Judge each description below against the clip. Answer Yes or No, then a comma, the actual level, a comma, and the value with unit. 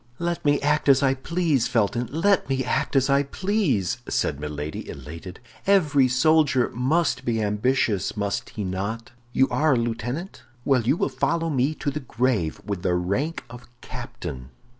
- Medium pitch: No, low, 130 Hz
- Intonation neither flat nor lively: No, wide, 6.0 semitones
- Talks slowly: No, average, 165 wpm